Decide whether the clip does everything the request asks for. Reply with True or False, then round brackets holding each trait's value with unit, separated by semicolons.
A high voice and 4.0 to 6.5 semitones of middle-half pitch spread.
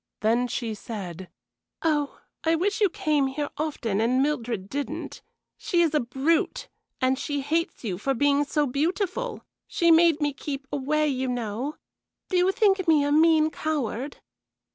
True (290 Hz; 4.3 semitones)